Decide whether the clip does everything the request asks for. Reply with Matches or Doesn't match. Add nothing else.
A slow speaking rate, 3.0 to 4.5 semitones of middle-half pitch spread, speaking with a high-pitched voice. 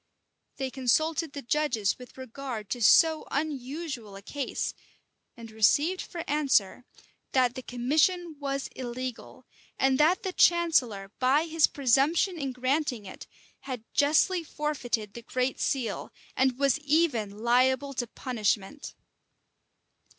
Matches